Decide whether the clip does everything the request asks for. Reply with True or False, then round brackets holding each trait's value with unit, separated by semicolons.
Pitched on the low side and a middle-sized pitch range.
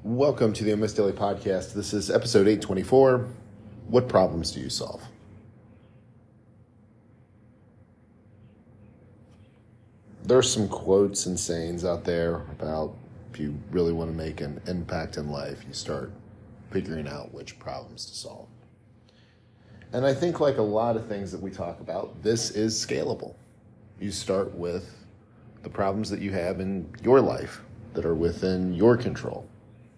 True (105 Hz; 3.2 semitones)